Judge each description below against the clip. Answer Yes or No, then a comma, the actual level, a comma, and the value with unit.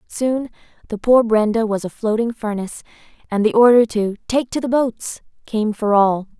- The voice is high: Yes, high, 225 Hz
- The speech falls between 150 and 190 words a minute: Yes, average, 180 wpm